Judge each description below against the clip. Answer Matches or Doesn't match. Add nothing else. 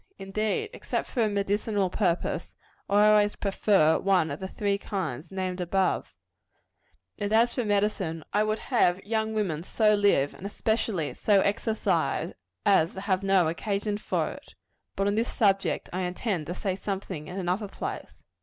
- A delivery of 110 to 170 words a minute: Matches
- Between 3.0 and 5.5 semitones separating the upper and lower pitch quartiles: Doesn't match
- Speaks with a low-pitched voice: Doesn't match